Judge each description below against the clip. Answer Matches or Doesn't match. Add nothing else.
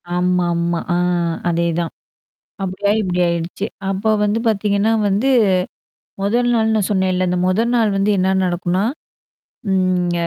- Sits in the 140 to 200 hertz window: Matches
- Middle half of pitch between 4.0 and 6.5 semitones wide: Doesn't match